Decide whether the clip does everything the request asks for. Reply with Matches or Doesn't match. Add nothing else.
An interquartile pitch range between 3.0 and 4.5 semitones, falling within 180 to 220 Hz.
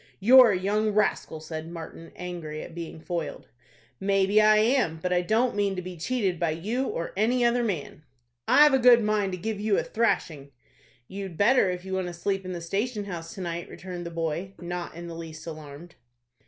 Matches